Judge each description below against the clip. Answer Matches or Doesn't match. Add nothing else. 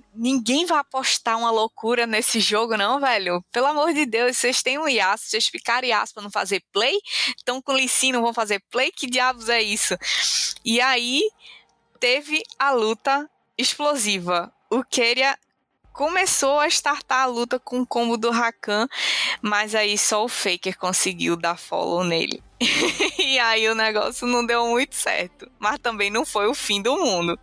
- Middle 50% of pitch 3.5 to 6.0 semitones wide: Matches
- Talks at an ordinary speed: Matches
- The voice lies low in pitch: Doesn't match